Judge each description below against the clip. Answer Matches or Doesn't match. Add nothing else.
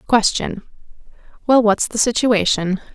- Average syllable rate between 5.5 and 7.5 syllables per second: Doesn't match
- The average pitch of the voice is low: Doesn't match